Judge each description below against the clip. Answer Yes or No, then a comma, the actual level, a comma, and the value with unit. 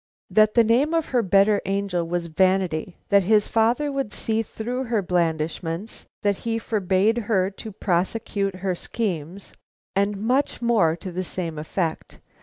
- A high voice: Yes, high, 200 Hz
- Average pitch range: Yes, average, 3.9 semitones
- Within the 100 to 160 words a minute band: Yes, average, 155 wpm